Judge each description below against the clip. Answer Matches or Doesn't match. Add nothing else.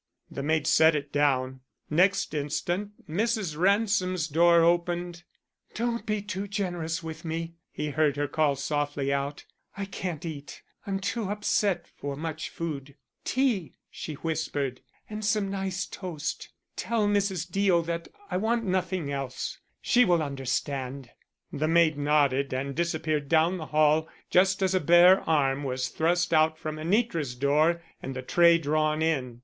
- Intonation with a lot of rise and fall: Doesn't match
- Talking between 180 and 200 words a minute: Doesn't match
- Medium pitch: Matches